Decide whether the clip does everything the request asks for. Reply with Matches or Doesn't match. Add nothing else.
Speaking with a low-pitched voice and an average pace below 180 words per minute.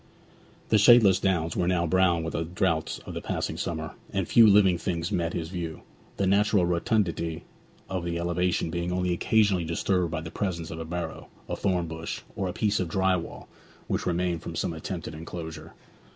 Doesn't match